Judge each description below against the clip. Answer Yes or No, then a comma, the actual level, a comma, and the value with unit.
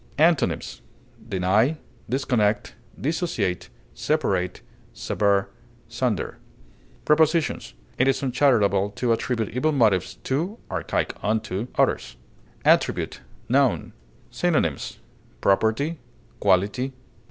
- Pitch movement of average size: No, wide, 6.3 semitones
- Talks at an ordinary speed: No, slow, 85 wpm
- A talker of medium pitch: No, low, 120 Hz